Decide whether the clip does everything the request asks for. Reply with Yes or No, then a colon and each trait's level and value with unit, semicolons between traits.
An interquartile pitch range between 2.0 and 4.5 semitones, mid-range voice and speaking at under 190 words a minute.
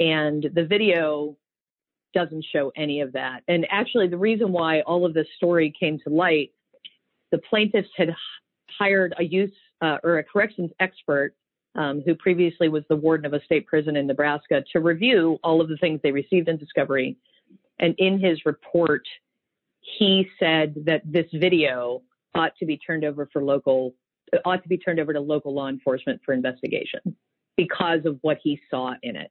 Yes: average, 3.2 semitones; medium, 160 Hz; average, 180 wpm